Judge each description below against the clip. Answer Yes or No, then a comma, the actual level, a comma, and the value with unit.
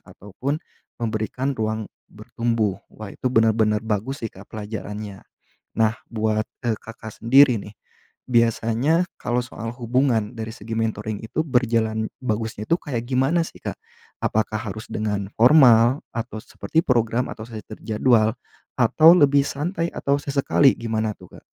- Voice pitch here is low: Yes, low, 115 Hz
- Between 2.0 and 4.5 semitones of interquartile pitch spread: Yes, average, 3.0 semitones